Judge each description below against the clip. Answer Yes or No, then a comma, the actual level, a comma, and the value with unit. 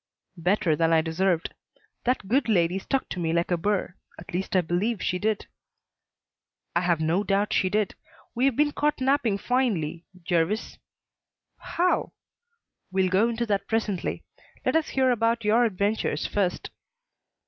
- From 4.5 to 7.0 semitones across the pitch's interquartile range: Yes, average, 4.9 semitones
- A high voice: Yes, high, 200 Hz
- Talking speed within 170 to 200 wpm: No, average, 155 wpm